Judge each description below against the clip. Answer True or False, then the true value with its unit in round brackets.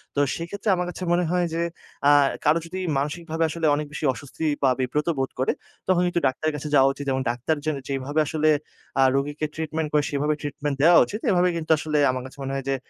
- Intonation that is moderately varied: True (3.2 semitones)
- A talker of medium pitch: True (150 Hz)